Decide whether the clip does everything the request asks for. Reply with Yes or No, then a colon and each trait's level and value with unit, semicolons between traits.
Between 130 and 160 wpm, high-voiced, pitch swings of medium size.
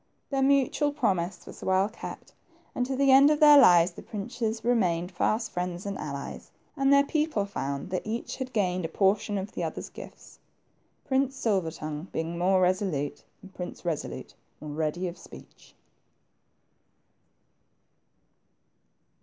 No: average, 145 wpm; high, 195 Hz; wide, 6.6 semitones